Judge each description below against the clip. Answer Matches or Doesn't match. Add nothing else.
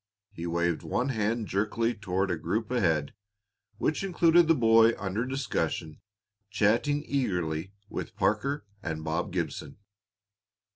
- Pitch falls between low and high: Doesn't match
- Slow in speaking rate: Matches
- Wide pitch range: Matches